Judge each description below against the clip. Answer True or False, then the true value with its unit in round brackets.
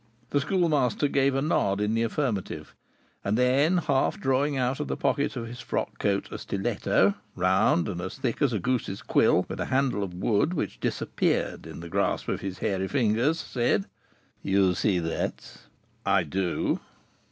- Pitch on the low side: True (115 Hz)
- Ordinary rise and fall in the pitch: False (5.9 semitones)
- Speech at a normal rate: True (175 wpm)